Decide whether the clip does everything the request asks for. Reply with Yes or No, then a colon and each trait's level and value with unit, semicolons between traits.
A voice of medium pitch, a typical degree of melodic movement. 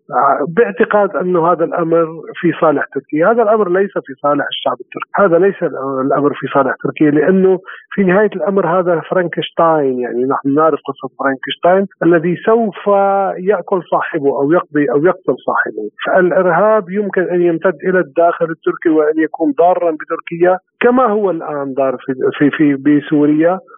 Yes: medium, 170 Hz; average, 4.9 semitones